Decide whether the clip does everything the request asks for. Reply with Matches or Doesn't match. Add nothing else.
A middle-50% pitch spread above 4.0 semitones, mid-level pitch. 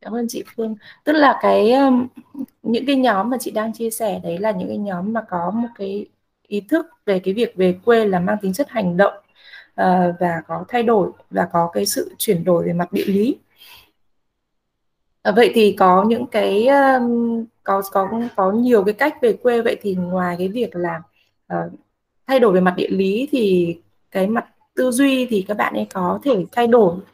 Doesn't match